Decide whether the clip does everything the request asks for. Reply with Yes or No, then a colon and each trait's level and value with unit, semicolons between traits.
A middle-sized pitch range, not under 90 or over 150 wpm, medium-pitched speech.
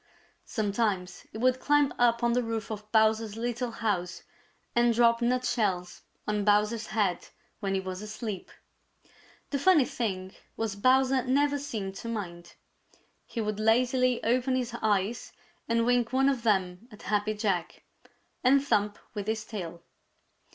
No: average, 3.2 semitones; average, 145 wpm; high, 225 Hz